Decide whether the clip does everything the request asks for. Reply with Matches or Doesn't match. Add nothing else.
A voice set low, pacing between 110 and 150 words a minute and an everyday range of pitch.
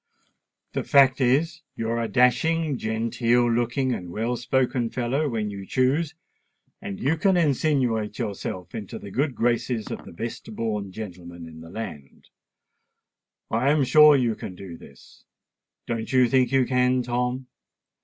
Matches